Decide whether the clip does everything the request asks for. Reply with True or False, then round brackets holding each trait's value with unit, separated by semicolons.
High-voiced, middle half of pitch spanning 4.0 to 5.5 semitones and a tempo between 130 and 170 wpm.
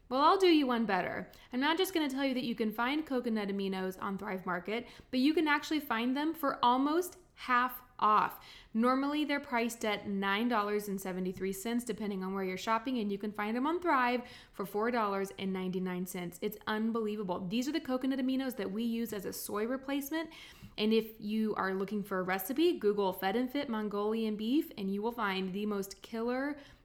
False (225 Hz; 4.7 semitones; 190 wpm)